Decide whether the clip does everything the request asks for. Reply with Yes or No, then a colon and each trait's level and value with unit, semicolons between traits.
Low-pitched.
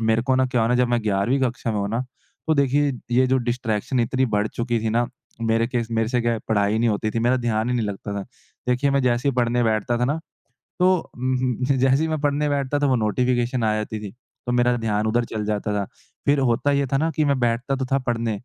Yes: low, 120 Hz